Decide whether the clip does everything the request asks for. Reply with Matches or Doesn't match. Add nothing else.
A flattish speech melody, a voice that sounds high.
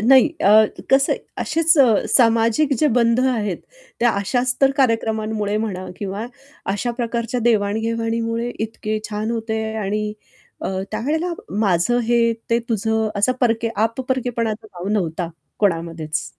Matches